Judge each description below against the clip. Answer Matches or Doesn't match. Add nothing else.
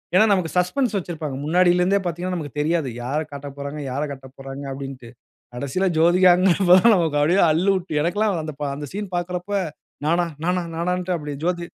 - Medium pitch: Matches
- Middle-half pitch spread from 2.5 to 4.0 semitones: Matches